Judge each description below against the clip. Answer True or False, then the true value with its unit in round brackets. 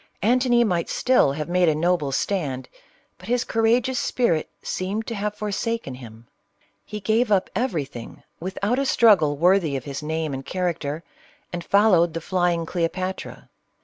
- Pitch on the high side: False (180 Hz)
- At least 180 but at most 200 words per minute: False (160 wpm)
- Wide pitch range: True (5.8 semitones)